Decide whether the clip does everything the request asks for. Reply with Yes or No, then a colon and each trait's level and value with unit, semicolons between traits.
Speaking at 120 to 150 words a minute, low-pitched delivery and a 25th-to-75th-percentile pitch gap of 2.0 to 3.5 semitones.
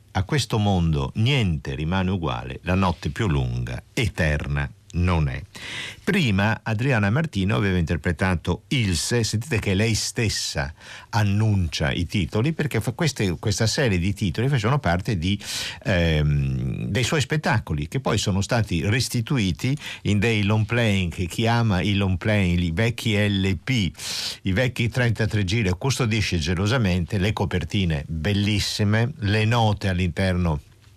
No: average, 135 wpm; low, 105 Hz; average, 4.3 semitones